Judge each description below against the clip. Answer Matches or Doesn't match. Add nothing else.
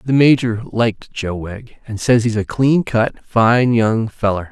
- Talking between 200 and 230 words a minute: Doesn't match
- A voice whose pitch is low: Matches